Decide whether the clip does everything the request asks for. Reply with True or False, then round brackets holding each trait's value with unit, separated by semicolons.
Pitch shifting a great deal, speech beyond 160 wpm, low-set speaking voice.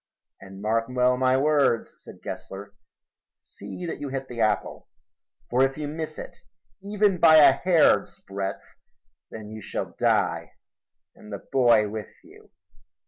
False (5.9 semitones; 145 wpm; 125 Hz)